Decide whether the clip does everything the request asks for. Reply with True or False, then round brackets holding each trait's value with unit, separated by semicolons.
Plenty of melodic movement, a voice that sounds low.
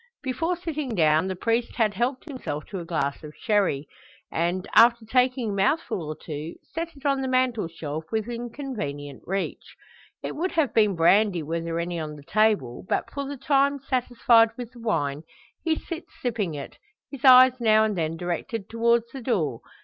False (7.4 semitones; 220 Hz)